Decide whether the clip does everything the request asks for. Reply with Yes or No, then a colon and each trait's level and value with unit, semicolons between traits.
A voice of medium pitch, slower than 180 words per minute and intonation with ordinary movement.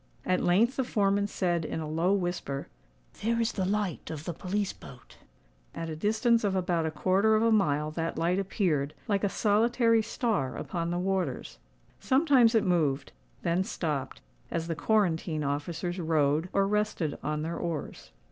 Yes: medium, 180 Hz; average, 165 wpm; average, 4.8 semitones